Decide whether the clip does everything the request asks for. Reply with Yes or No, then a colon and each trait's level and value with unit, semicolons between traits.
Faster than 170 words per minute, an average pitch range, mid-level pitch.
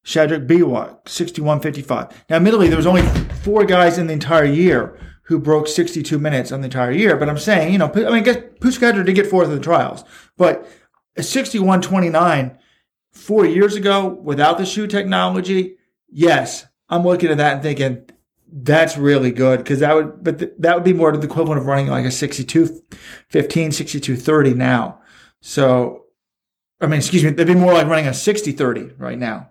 Yes: average, 185 wpm; average, 4.2 semitones; medium, 160 Hz